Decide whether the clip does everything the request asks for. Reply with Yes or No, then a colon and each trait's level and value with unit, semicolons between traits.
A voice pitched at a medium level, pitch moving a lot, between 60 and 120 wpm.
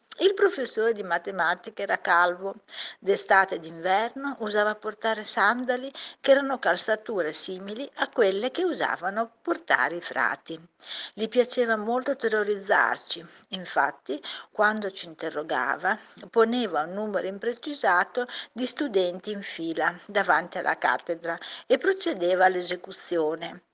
No: high, 210 Hz; wide, 5.7 semitones; slow, 115 wpm